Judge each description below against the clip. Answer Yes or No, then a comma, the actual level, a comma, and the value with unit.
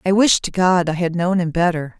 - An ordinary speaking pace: No, fast, 270 wpm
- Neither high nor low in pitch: Yes, medium, 175 Hz